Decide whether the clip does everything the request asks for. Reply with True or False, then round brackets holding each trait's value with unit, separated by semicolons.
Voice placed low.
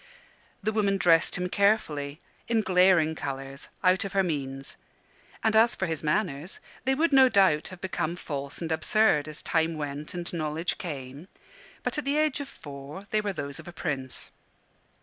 False (170 Hz)